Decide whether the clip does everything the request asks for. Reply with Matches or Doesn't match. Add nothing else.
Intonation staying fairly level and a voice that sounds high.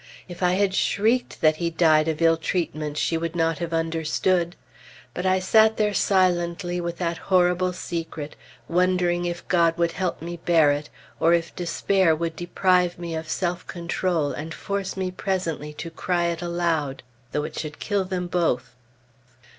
Doesn't match